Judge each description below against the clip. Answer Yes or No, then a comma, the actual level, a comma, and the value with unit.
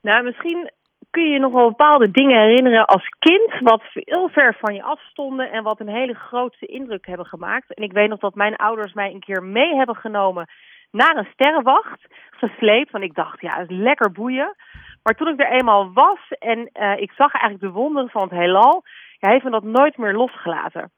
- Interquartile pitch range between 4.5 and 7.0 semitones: Yes, average, 5.1 semitones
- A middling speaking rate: No, fast, 215 wpm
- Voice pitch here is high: Yes, high, 230 Hz